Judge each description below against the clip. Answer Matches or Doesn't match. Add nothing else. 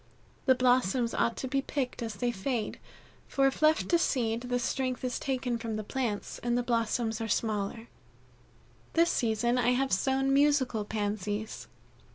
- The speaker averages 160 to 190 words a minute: Matches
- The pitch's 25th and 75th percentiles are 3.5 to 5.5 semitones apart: Doesn't match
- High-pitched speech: Matches